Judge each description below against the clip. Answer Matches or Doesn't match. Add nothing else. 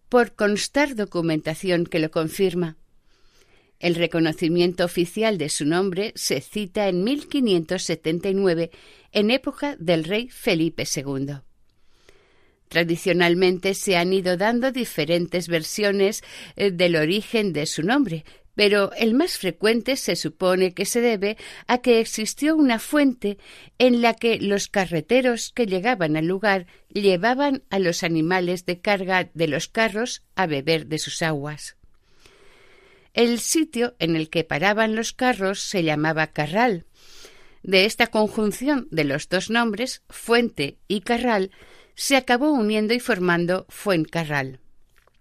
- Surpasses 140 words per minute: Doesn't match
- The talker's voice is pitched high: Matches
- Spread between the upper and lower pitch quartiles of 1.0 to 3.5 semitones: Doesn't match